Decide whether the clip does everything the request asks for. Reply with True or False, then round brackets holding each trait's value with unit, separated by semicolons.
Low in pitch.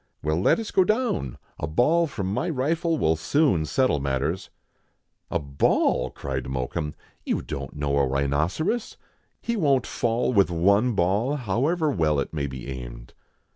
True (95 Hz)